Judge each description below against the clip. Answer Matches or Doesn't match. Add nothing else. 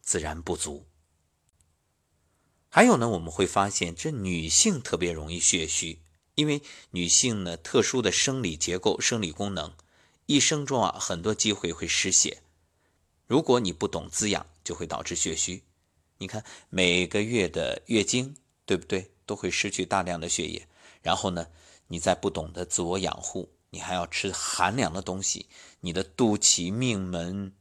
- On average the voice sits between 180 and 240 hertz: Doesn't match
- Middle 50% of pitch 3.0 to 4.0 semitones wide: Matches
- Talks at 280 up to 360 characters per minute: Doesn't match